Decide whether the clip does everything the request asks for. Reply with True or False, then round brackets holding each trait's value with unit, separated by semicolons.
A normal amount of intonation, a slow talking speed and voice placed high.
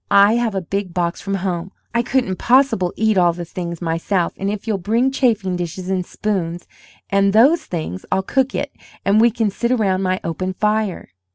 False (3.8 semitones; 195 wpm; 195 Hz)